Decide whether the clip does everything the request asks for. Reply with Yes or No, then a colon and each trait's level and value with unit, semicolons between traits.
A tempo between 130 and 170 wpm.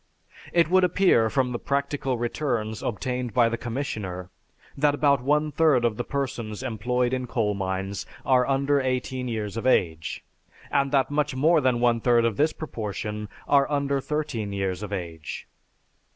Yes: average, 165 wpm